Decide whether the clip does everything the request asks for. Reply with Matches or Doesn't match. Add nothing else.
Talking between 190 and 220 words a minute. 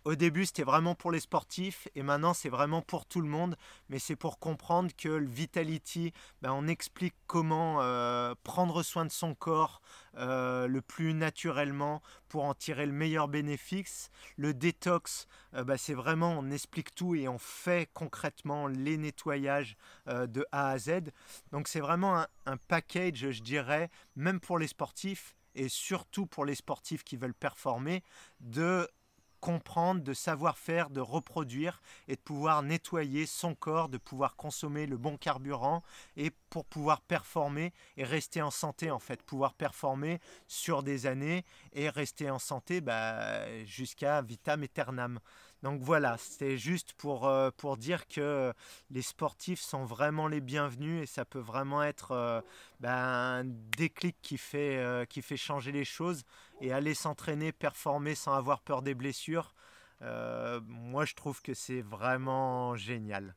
Doesn't match